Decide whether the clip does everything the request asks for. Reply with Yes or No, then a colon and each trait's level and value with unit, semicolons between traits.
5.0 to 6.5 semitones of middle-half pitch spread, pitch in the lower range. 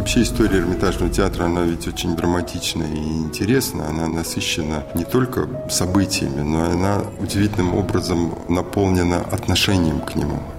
No: average, 3.1 semitones; very low, 85 Hz